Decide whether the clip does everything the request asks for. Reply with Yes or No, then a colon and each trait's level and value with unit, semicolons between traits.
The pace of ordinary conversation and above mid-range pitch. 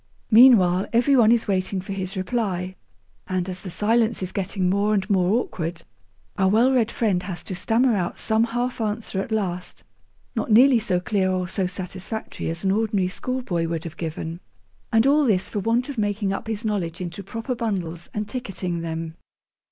Yes: average, 185 wpm; high, 195 Hz